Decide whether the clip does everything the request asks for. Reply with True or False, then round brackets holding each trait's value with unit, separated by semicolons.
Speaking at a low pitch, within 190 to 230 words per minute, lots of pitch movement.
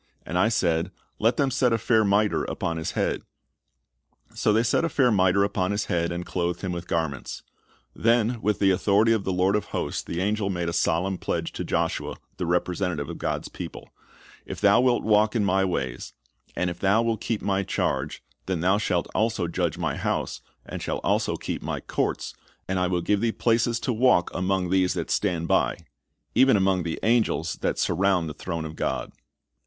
False (95 Hz; 200 wpm; 3.8 semitones)